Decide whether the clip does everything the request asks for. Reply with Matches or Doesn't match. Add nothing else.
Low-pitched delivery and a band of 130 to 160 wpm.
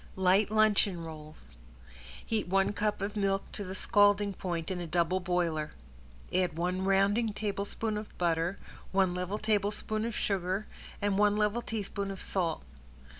Doesn't match